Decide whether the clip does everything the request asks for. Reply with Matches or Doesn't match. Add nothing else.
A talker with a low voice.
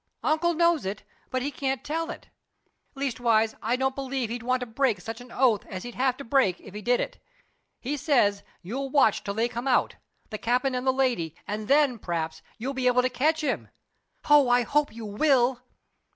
Doesn't match